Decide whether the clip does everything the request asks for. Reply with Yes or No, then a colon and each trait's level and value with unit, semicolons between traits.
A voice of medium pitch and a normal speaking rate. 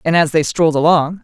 No: medium, 160 Hz; fast, 245 wpm